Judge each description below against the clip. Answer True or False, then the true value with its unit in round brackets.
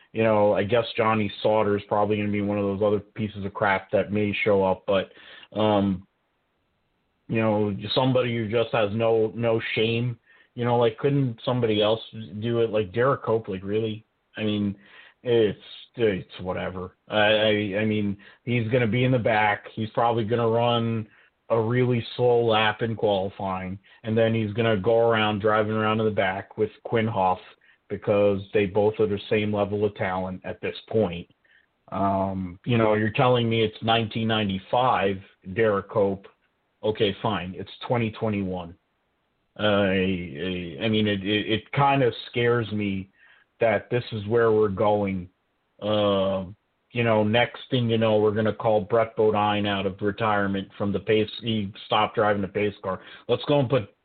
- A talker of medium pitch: False (105 Hz)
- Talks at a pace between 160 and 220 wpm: True (175 wpm)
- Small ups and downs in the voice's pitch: True (2.2 semitones)